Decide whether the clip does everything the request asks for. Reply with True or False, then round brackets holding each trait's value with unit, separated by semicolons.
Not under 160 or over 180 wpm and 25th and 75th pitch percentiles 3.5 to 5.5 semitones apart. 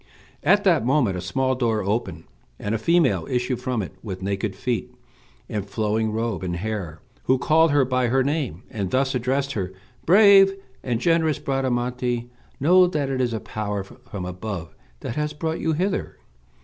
True (175 wpm; 5.2 semitones)